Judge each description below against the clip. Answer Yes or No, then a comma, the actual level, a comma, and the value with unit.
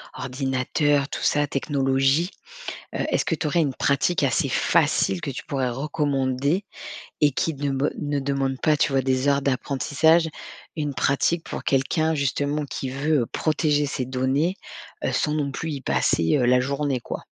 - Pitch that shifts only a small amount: Yes, narrow, 2.1 semitones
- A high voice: No, medium, 140 Hz